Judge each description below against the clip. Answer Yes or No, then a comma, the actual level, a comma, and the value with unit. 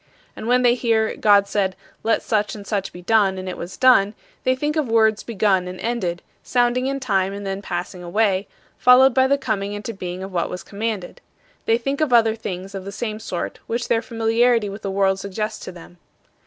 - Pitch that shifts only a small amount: No, average, 3.5 semitones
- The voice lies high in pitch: Yes, high, 215 Hz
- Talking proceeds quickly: Yes, fast, 210 wpm